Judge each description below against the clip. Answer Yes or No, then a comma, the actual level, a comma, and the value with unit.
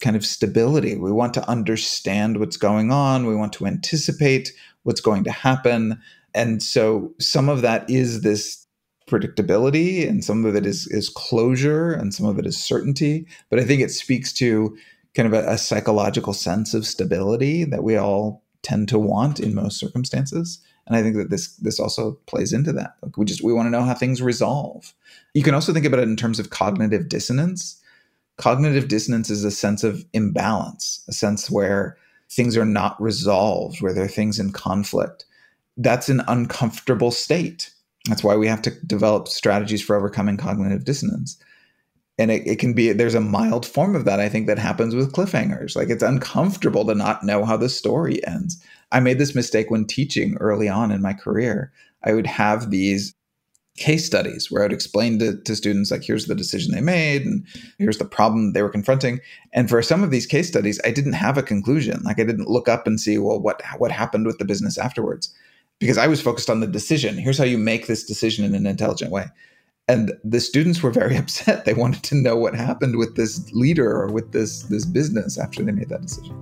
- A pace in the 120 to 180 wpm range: No, fast, 205 wpm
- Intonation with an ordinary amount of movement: Yes, average, 4.4 semitones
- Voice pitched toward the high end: No, low, 115 Hz